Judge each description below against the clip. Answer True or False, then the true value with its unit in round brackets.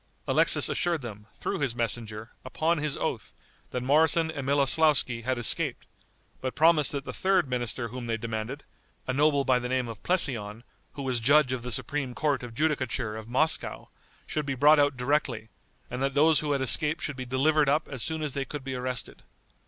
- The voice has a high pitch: False (135 Hz)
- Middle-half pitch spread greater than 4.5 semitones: False (3.5 semitones)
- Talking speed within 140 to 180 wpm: False (195 wpm)